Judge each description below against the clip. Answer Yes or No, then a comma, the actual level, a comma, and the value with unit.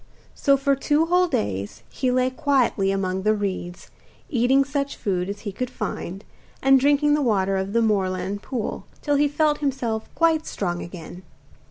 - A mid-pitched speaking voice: No, high, 235 Hz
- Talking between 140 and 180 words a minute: Yes, average, 170 wpm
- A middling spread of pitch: No, wide, 6.4 semitones